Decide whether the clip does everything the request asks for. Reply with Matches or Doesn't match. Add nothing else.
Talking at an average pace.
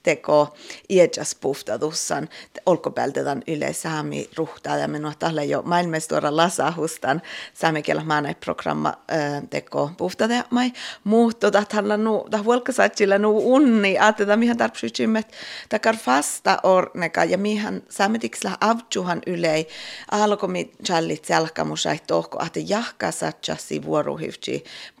Doesn't match